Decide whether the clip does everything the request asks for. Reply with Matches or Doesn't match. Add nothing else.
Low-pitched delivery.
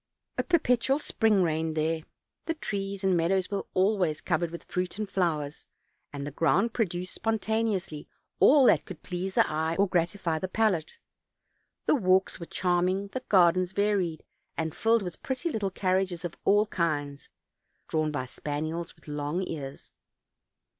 Doesn't match